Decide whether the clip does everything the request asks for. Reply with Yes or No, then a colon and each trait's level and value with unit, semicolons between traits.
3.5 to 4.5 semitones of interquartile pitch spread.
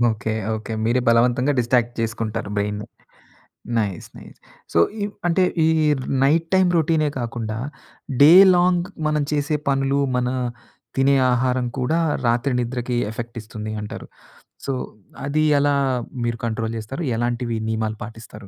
Yes: average, 4.1 semitones